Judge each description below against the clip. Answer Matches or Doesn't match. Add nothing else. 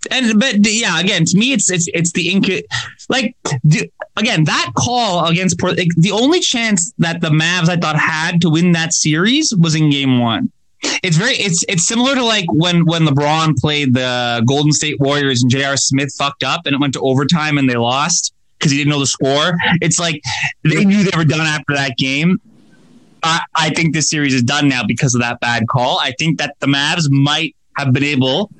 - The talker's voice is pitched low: Doesn't match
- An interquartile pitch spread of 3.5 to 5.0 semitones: Matches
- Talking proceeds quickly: Matches